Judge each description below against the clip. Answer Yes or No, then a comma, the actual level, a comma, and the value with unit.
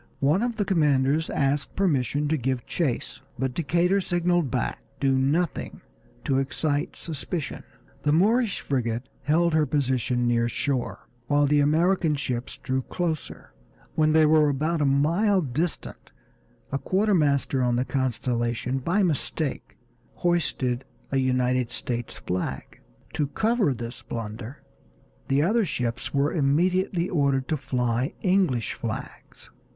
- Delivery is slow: Yes, slow, 130 wpm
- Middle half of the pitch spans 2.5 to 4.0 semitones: No, average, 4.8 semitones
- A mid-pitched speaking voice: Yes, medium, 145 Hz